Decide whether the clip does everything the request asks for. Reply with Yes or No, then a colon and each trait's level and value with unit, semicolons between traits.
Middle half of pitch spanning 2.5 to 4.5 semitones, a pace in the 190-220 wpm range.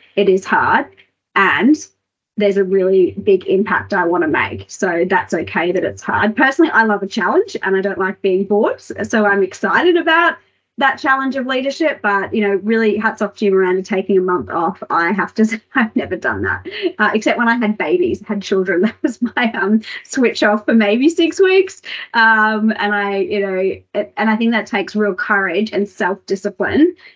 Yes: average, 4.0 semitones; fast, 205 wpm